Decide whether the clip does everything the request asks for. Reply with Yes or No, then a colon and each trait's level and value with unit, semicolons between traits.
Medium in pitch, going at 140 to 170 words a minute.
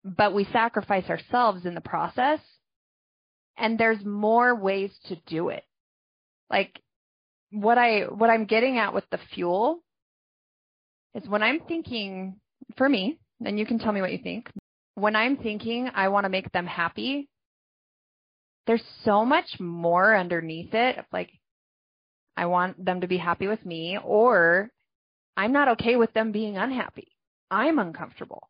No: high, 210 Hz; average, 155 wpm